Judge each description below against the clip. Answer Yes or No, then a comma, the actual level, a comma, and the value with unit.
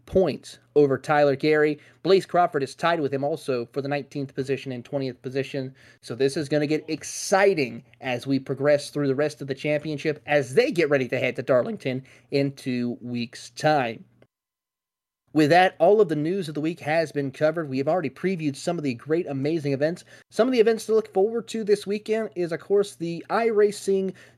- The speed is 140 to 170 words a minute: No, fast, 205 wpm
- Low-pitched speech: No, medium, 150 Hz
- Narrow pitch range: No, average, 4.4 semitones